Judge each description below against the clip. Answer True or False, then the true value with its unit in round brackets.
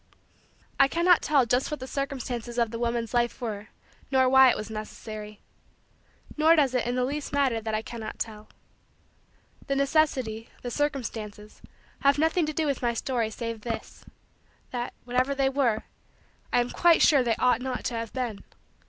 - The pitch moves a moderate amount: True (3.3 semitones)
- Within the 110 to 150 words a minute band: False (175 wpm)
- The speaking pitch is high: True (245 Hz)